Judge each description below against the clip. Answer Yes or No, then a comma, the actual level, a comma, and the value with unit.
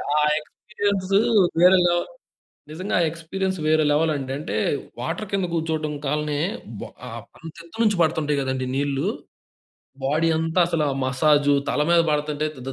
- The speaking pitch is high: No, medium, 155 Hz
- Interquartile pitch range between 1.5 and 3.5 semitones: Yes, average, 3.0 semitones